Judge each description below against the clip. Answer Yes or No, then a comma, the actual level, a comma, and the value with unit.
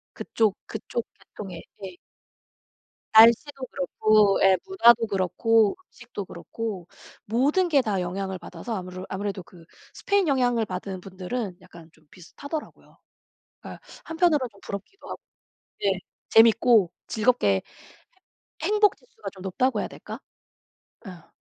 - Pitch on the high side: Yes, high, 215 Hz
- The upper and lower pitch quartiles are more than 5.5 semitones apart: No, average, 5.1 semitones